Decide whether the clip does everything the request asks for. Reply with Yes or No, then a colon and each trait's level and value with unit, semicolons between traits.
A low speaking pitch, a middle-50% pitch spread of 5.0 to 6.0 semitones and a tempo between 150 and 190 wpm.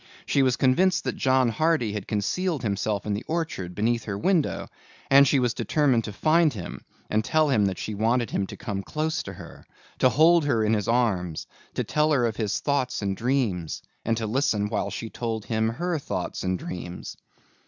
No: low, 115 Hz; wide, 5.4 semitones; average, 200 wpm